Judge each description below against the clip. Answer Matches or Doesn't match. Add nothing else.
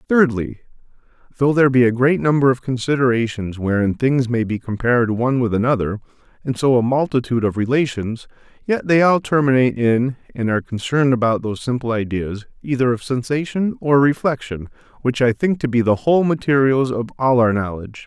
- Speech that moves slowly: Doesn't match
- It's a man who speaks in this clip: Matches